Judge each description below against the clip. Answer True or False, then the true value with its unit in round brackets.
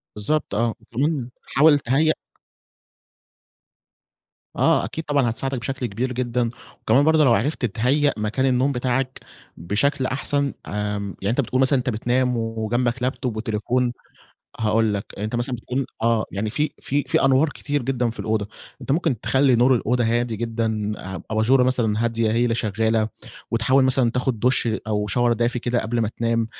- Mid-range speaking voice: False (120 Hz)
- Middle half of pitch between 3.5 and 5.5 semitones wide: False (2.9 semitones)